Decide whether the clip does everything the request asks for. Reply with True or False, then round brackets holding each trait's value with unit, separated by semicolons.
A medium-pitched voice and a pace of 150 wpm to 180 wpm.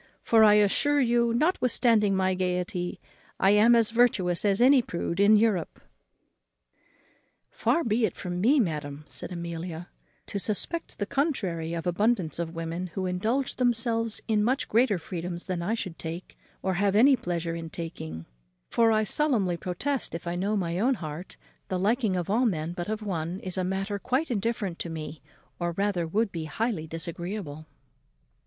False (195 Hz; 170 wpm)